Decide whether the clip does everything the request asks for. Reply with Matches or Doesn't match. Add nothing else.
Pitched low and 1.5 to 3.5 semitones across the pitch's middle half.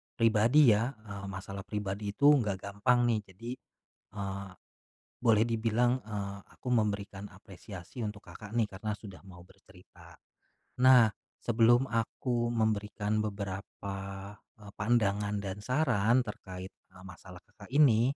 Matches